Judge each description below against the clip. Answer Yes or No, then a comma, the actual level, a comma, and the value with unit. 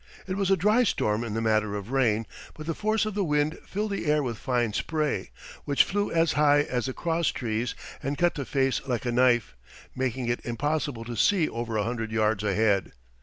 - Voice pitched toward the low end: Yes, low, 130 Hz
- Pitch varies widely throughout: Yes, wide, 5.9 semitones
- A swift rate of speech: Yes, fast, 210 wpm